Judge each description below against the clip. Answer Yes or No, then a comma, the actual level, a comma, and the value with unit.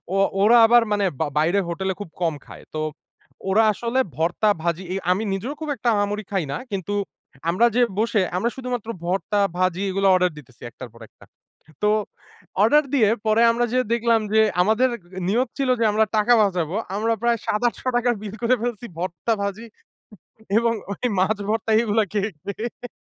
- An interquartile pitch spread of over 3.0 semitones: Yes, average, 3.7 semitones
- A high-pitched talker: Yes, high, 215 Hz